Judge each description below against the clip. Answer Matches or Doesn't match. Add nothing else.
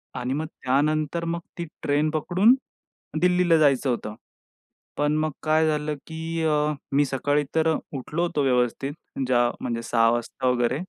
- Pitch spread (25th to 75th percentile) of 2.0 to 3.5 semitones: Doesn't match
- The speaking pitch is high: Doesn't match